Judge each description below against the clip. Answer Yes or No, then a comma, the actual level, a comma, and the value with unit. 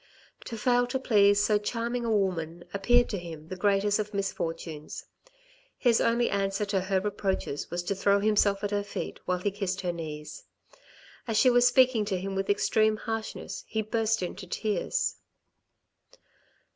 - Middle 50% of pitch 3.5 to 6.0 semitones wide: No, average, 2.8 semitones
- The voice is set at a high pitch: Yes, high, 205 Hz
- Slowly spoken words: No, average, 165 wpm